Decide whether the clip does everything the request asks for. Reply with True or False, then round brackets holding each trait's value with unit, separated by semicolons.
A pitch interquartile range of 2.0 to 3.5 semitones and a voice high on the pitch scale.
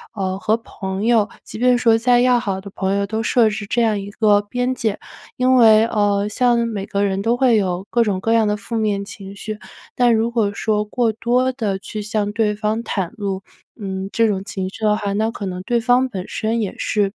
True (2.6 semitones; 215 Hz)